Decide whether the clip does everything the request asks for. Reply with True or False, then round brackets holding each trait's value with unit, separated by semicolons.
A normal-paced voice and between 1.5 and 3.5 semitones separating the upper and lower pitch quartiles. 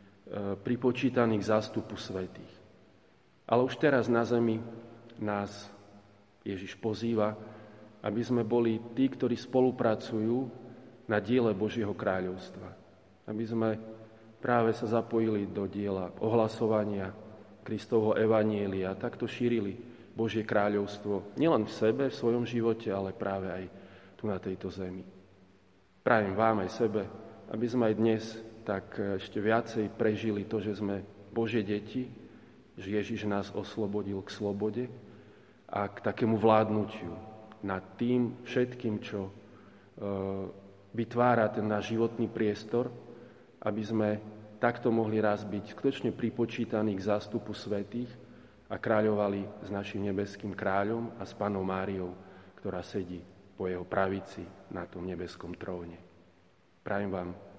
True (125 wpm; 2.6 semitones)